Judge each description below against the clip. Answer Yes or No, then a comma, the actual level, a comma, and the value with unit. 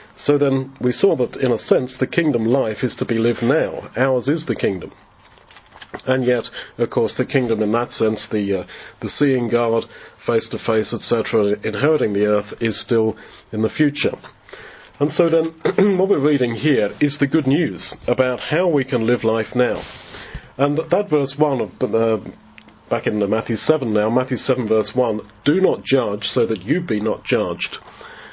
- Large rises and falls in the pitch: No, average, 4.2 semitones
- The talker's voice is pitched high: No, low, 125 Hz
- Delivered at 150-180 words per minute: No, average, 190 wpm